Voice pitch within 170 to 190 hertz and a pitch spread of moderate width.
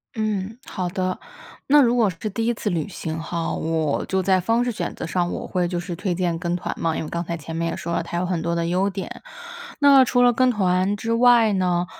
Yes: medium, 185 Hz; average, 4.6 semitones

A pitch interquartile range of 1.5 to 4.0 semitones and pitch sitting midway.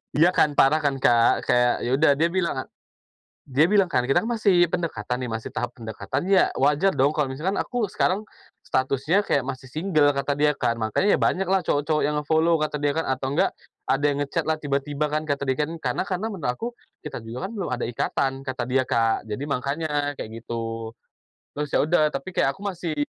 No: average, 4.4 semitones; medium, 145 Hz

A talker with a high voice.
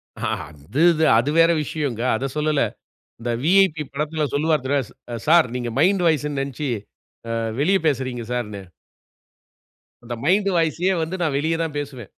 No: medium, 150 Hz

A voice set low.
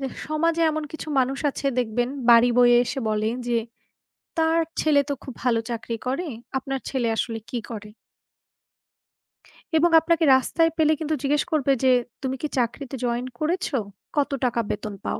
No: very high, 270 Hz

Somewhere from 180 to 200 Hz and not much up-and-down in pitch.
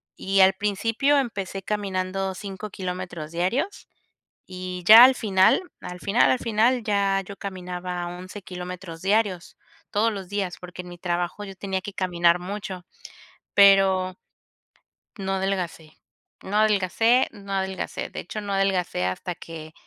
Yes: high, 190 Hz; narrow, 2.2 semitones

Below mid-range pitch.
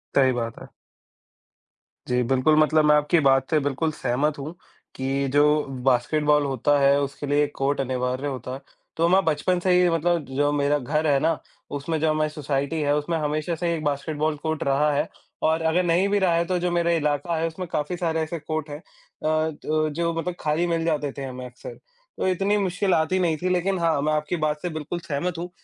No: medium, 155 Hz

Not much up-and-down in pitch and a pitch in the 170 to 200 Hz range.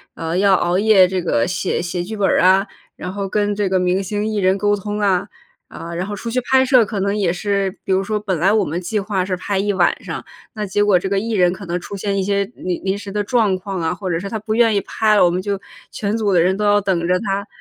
Yes: narrow, 2.1 semitones; high, 195 Hz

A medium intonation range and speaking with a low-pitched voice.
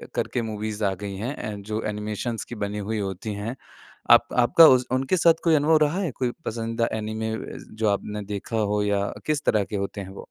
Yes: average, 3.2 semitones; low, 110 Hz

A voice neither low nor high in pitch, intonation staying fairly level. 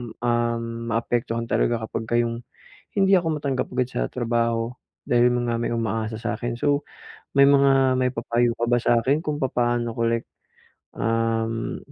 No: low, 120 Hz; narrow, 1.8 semitones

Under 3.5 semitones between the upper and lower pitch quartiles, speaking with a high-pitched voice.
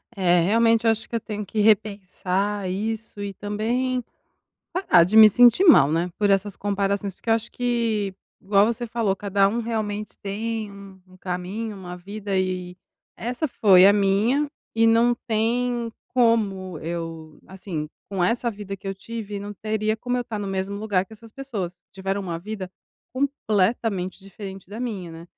Yes: average, 3.0 semitones; high, 205 Hz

